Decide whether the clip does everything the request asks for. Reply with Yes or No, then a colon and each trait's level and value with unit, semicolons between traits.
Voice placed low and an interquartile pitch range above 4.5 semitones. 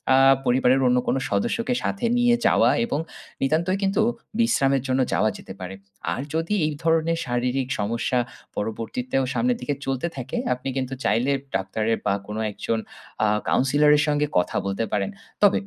Yes: low, 130 Hz; wide, 5.4 semitones